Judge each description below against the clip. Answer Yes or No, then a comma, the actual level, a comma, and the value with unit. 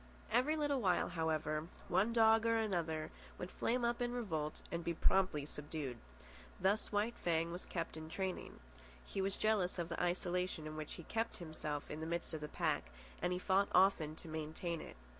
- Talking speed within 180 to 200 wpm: Yes, average, 190 wpm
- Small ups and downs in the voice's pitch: No, average, 4.5 semitones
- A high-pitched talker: No, medium, 175 Hz